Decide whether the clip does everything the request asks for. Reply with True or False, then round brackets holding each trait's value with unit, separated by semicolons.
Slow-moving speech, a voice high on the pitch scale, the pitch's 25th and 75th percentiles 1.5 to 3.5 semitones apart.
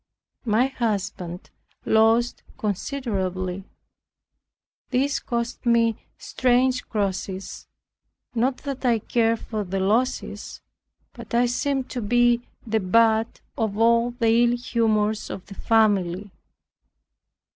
True (105 wpm; 230 Hz; 2.7 semitones)